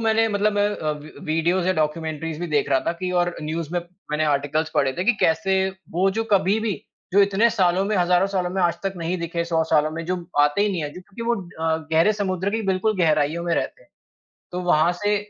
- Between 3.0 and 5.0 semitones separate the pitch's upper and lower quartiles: Yes, average, 3.6 semitones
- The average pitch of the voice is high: No, medium, 175 Hz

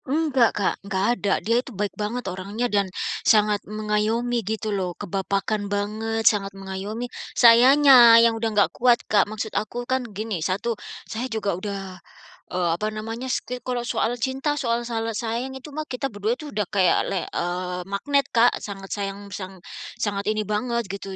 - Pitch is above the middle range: Yes, high, 215 Hz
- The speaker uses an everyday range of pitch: Yes, average, 3.1 semitones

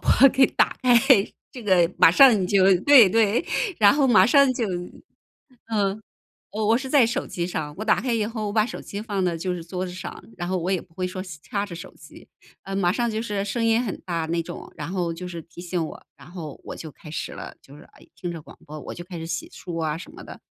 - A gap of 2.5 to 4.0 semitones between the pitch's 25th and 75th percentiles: No, average, 4.6 semitones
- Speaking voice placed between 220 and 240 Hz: No, high, 190 Hz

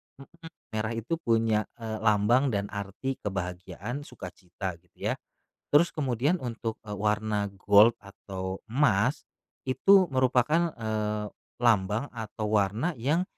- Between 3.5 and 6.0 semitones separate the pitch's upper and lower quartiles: Yes, average, 4.2 semitones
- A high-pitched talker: No, low, 110 Hz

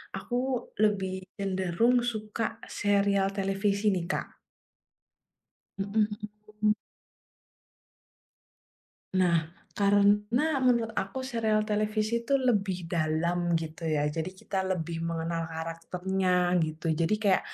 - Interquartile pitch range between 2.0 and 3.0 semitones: No, average, 4.0 semitones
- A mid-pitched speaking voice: No, high, 195 Hz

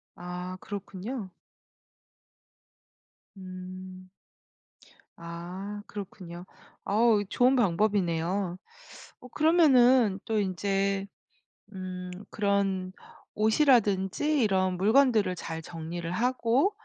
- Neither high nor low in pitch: No, high, 195 Hz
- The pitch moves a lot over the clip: No, average, 3.4 semitones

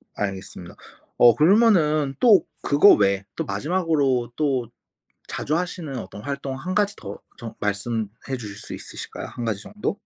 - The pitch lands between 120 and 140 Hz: Yes, low, 135 Hz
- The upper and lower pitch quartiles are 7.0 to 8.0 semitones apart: Yes, wide, 7.5 semitones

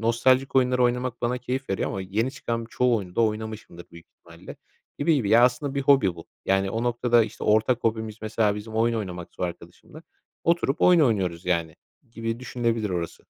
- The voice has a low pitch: Yes, low, 115 Hz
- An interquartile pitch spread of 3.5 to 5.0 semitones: Yes, average, 3.9 semitones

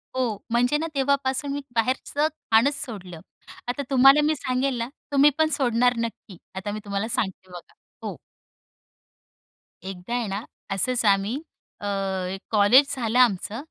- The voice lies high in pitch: Yes, high, 240 Hz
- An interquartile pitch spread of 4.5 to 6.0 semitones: Yes, average, 4.9 semitones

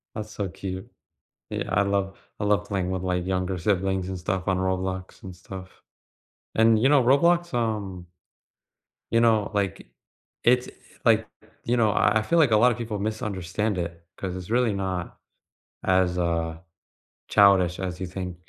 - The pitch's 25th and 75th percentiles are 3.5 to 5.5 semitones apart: No, average, 2.9 semitones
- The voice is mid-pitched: No, very low, 95 Hz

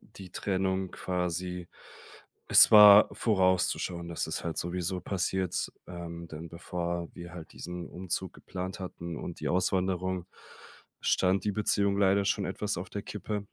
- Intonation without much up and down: Yes, narrow, 1.6 semitones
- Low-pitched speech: Yes, very low, 90 Hz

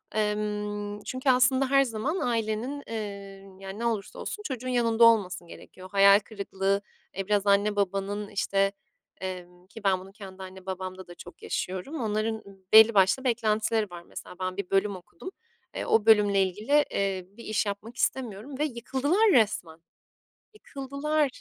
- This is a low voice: No, high, 210 Hz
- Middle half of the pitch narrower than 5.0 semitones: Yes, average, 3.3 semitones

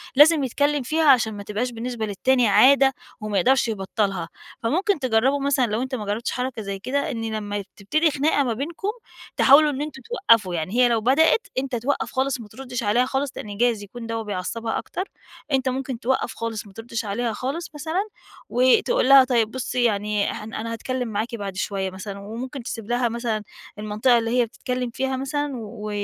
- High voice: Yes, high, 240 Hz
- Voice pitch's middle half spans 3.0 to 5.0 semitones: Yes, average, 3.9 semitones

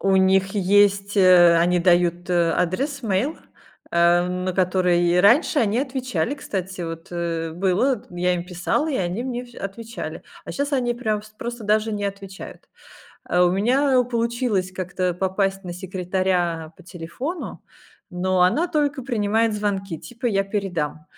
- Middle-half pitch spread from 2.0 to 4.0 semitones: No, average, 4.6 semitones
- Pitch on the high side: Yes, high, 195 Hz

